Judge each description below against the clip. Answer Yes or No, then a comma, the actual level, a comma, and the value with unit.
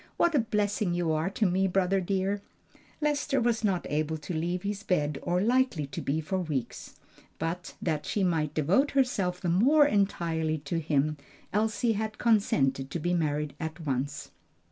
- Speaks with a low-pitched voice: No, medium, 180 Hz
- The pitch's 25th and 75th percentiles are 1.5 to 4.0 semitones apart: No, average, 5.1 semitones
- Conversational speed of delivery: Yes, average, 170 wpm